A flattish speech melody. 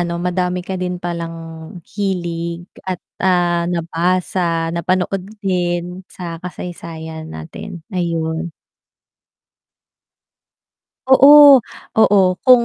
Yes: narrow, 1.5 semitones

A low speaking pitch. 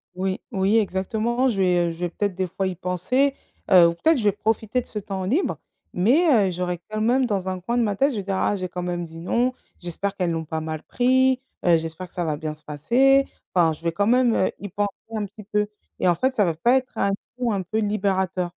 No: high, 195 Hz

